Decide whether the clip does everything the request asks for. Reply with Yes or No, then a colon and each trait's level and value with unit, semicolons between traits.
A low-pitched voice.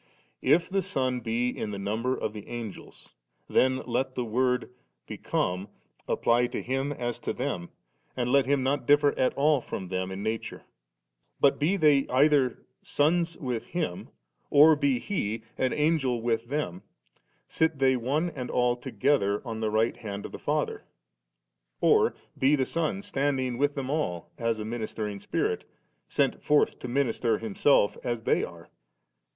Yes: low, 125 Hz